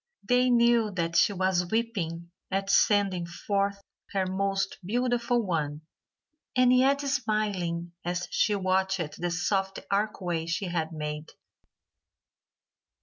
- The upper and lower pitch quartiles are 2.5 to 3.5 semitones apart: No, average, 4.0 semitones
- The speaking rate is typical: No, slow, 115 wpm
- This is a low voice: No, high, 195 Hz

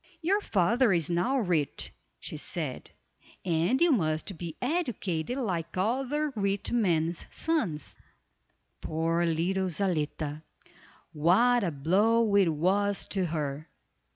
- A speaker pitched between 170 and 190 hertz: Yes, medium, 185 Hz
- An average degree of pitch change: No, wide, 6.1 semitones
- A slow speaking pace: Yes, slow, 115 wpm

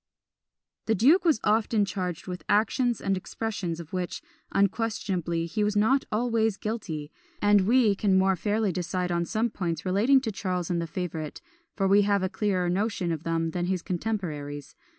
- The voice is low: No, high, 195 Hz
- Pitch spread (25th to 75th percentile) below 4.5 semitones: Yes, average, 3.8 semitones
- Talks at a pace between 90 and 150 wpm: No, average, 175 wpm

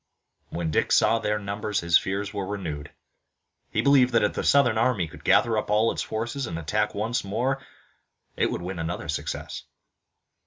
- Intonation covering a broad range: No, average, 4.5 semitones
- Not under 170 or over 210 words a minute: Yes, average, 180 wpm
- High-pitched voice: No, low, 105 Hz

